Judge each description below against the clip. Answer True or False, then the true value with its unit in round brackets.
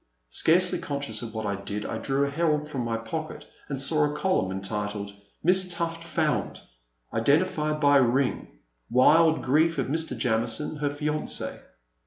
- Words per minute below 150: False (160 wpm)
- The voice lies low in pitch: False (145 Hz)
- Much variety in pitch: True (5.7 semitones)